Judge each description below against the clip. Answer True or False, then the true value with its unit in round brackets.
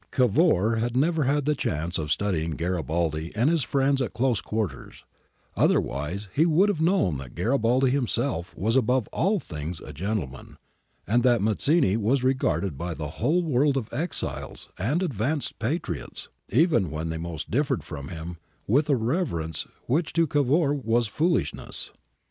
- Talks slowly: False (155 wpm)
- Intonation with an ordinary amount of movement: False (8.7 semitones)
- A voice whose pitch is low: True (120 Hz)